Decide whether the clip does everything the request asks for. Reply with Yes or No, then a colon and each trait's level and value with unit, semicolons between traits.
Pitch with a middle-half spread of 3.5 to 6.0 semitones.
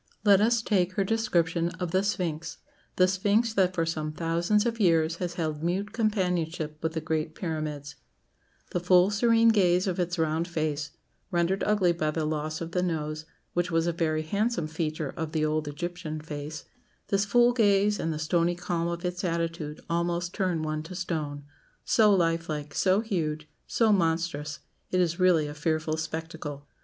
No: average, 3.0 semitones